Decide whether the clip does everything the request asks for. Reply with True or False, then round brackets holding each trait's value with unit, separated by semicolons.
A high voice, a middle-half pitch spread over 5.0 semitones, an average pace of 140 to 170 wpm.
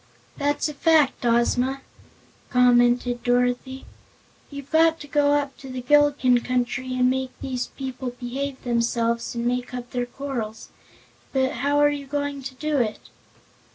False (260 Hz; 2.6 semitones; 150 wpm)